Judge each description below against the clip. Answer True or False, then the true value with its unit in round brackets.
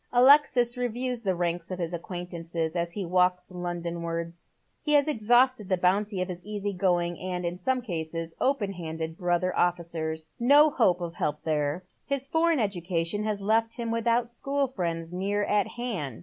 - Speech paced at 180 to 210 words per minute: False (165 wpm)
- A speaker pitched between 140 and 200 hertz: True (185 Hz)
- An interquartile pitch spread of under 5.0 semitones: False (5.4 semitones)